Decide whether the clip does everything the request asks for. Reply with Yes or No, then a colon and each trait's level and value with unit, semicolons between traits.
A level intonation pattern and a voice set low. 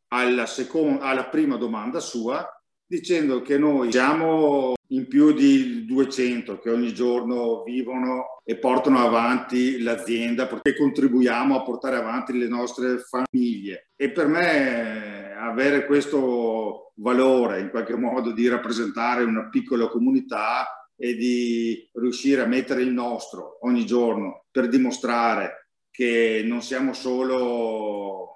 Yes: narrow, 2.3 semitones; low, 125 Hz